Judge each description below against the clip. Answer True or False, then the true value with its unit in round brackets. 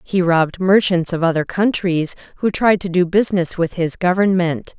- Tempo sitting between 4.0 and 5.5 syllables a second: True (5.0 syllables/s)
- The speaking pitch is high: False (180 Hz)